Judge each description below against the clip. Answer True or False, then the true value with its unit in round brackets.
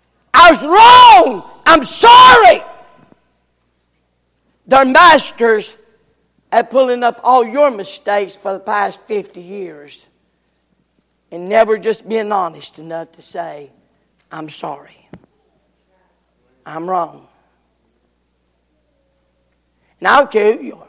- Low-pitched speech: False (200 Hz)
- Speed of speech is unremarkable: False (100 wpm)